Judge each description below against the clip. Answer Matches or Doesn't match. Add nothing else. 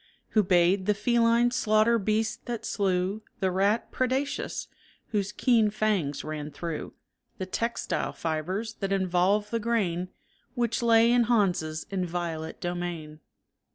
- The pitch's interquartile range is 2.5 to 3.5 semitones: Doesn't match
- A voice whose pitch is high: Matches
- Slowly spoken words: Matches